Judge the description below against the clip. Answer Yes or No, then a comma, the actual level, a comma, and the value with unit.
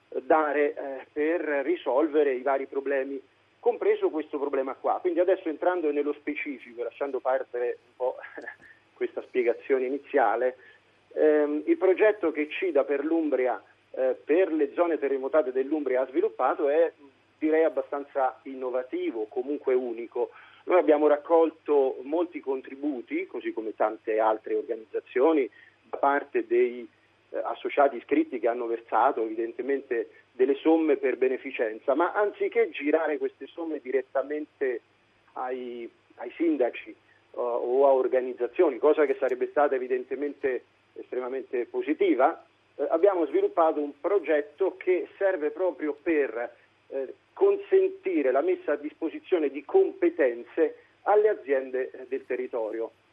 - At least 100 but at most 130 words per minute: Yes, average, 120 wpm